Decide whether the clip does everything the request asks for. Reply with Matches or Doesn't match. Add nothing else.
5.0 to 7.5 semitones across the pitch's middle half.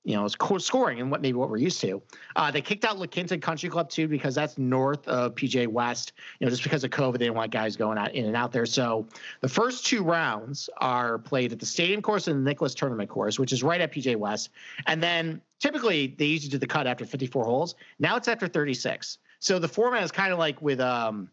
Matches